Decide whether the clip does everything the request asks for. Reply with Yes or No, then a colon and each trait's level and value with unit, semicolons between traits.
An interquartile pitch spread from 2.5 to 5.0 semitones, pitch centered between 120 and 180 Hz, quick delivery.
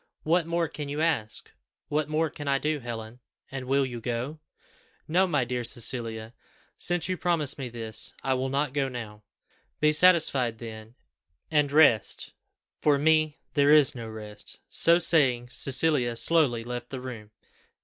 No: average, 4.4 semitones; low, 135 Hz; average, 160 wpm